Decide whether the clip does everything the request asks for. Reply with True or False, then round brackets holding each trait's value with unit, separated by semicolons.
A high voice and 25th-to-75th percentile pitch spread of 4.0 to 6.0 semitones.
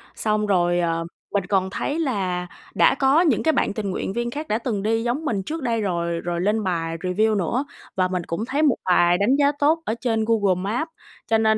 True (215 Hz; 5.1 semitones)